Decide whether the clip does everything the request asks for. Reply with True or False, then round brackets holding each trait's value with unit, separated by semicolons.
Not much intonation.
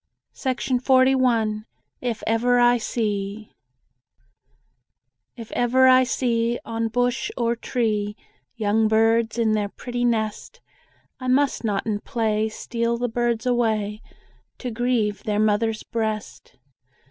True (2.1 semitones)